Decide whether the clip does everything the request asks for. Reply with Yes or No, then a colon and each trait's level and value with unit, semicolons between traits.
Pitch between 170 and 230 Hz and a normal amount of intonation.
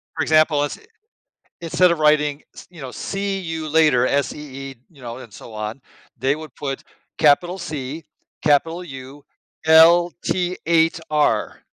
No: medium, 150 Hz; average, 3.4 semitones